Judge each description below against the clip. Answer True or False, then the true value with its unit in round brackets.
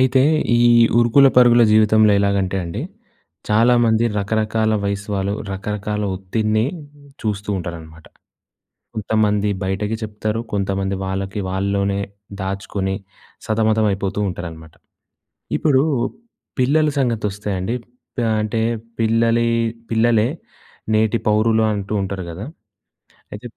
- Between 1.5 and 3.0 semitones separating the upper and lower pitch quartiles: True (2.4 semitones)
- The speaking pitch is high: False (105 Hz)